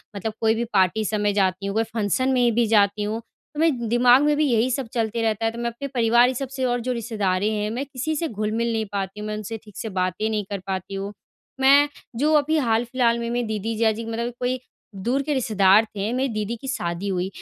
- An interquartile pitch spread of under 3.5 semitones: Yes, average, 2.9 semitones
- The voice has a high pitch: Yes, high, 225 Hz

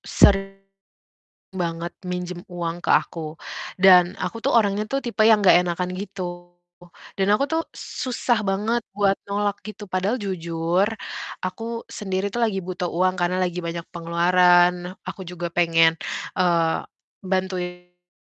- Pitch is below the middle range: No, medium, 185 Hz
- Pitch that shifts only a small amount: Yes, narrow, 2.2 semitones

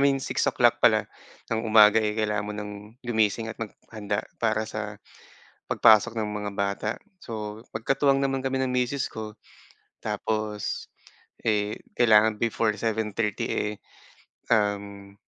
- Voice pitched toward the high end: No, low, 110 Hz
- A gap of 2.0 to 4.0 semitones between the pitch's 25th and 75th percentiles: No, narrow, 1.5 semitones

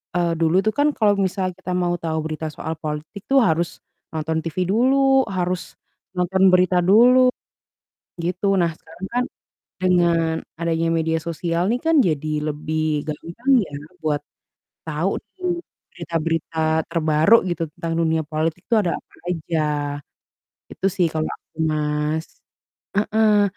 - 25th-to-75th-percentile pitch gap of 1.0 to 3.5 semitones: Yes, average, 3.1 semitones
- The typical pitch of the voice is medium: Yes, medium, 170 Hz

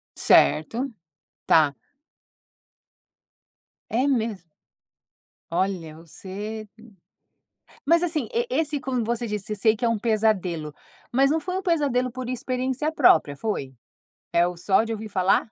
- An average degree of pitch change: No, wide, 5.7 semitones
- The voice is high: Yes, high, 225 Hz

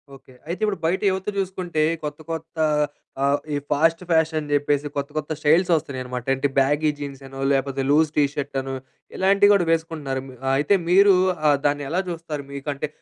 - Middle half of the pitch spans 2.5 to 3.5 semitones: Yes, average, 2.9 semitones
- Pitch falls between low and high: Yes, medium, 150 Hz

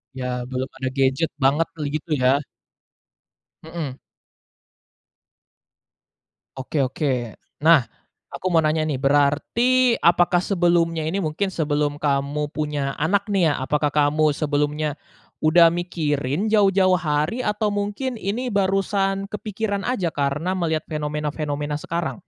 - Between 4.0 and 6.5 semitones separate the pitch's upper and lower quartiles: Yes, average, 4.5 semitones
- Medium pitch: Yes, medium, 155 Hz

